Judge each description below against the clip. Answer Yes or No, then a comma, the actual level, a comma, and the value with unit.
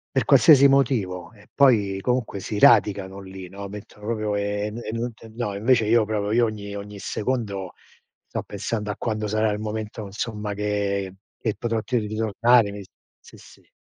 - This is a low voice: Yes, low, 105 Hz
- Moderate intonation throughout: No, narrow, 2.1 semitones